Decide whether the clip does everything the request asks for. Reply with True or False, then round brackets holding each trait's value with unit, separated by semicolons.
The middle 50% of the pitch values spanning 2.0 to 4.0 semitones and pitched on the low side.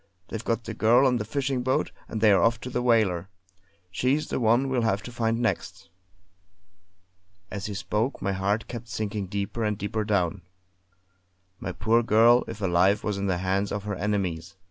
True (3.1 semitones; 110 Hz)